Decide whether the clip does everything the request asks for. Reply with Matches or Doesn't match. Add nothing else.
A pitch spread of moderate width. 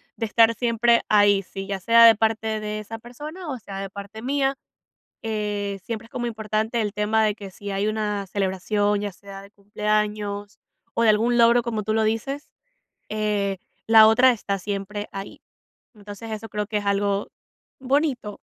Doesn't match